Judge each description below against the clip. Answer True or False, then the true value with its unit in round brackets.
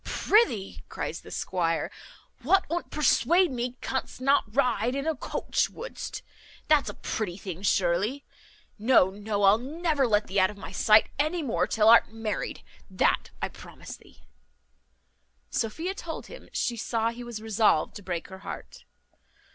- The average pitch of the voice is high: True (230 Hz)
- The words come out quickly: False (155 wpm)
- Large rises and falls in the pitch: True (5.8 semitones)